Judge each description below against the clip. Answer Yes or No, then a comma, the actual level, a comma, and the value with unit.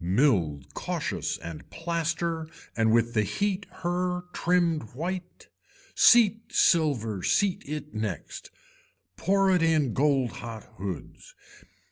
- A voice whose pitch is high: No, medium, 155 Hz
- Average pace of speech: No, slow, 110 wpm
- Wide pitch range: Yes, wide, 8.1 semitones